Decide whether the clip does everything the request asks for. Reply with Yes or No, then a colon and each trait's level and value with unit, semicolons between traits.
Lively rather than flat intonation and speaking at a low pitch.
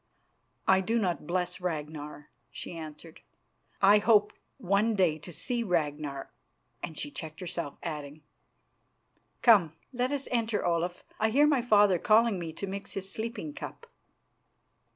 No: wide, 5.7 semitones; medium, 185 Hz